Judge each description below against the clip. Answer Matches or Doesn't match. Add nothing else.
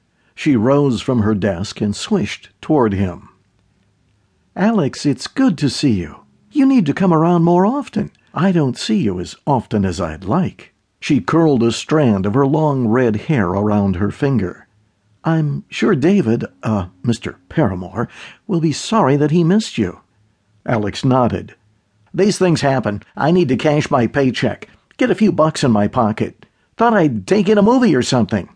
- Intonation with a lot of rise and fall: Matches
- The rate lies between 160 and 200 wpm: Matches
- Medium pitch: Doesn't match